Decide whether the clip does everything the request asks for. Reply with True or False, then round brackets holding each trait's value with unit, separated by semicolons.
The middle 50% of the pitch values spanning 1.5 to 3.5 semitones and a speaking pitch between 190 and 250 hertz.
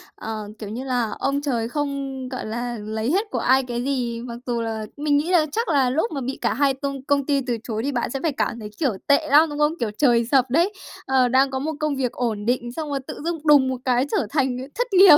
False (3.2 semitones; 265 Hz)